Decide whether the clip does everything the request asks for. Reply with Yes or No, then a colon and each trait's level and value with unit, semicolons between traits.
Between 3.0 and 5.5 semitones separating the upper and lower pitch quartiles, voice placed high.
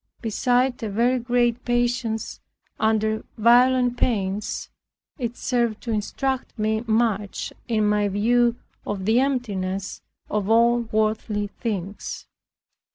No: narrow, 2.5 semitones; high, 225 Hz